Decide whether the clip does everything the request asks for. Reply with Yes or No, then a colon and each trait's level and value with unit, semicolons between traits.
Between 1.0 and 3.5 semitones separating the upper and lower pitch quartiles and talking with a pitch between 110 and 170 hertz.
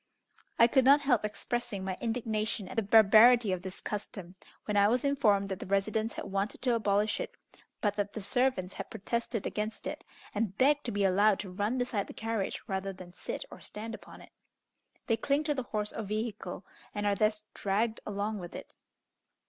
No: average, 2.8 semitones; high, 215 Hz